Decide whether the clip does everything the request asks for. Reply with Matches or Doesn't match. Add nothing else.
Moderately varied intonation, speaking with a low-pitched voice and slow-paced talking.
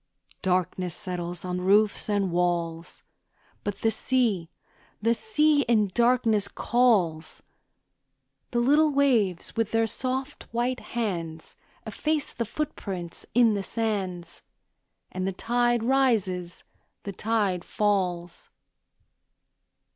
Doesn't match